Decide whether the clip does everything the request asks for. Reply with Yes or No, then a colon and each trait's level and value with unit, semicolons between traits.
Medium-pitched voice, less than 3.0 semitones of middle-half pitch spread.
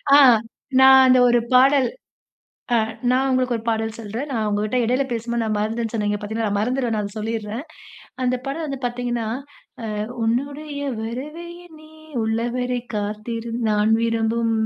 No: high, 235 Hz; narrow, 2.5 semitones